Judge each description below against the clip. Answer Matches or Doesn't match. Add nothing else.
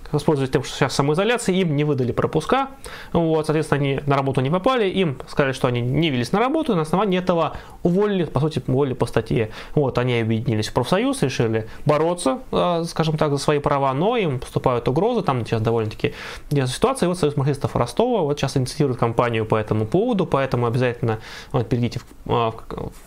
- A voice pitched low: Doesn't match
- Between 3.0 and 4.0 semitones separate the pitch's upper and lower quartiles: Doesn't match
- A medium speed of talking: Doesn't match